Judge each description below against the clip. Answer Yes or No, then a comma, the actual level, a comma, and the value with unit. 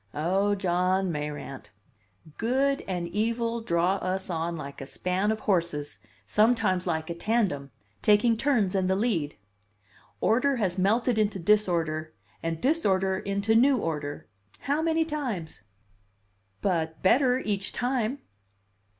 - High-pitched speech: Yes, high, 195 Hz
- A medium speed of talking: No, slow, 125 wpm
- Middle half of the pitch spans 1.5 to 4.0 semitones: No, average, 5.3 semitones